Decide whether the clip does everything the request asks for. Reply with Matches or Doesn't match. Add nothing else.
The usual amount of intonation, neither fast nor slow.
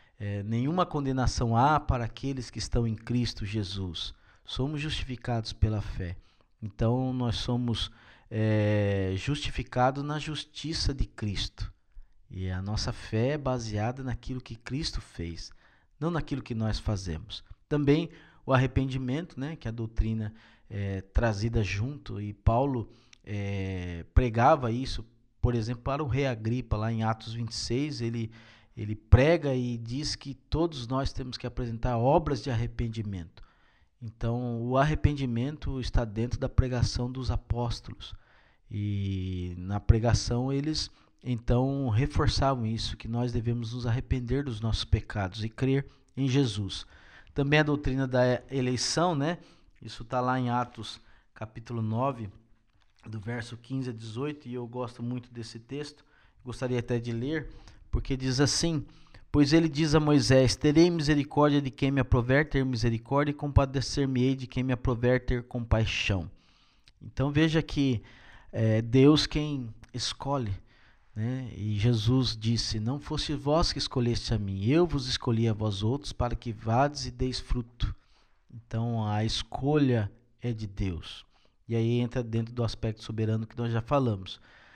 Matches